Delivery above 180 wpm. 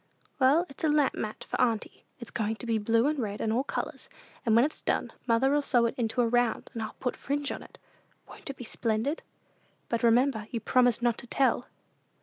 Yes: fast, 205 wpm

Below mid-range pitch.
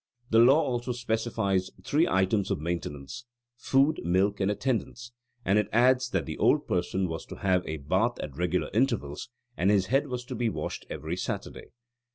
Yes: low, 105 Hz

